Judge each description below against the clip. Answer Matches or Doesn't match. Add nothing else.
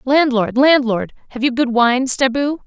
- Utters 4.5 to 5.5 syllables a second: Doesn't match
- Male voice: Doesn't match